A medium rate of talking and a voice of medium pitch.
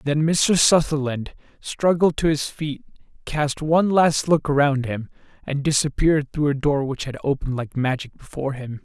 Yes: average, 170 wpm; medium, 145 Hz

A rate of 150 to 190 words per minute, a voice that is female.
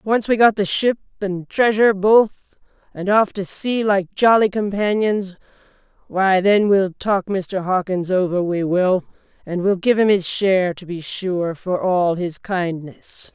Yes: average, 165 wpm; female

